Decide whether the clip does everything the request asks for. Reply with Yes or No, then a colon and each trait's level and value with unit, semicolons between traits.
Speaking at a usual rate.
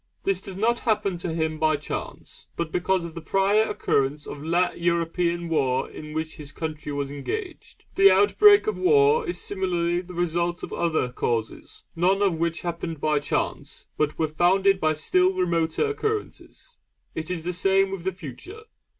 Yes: average, 175 wpm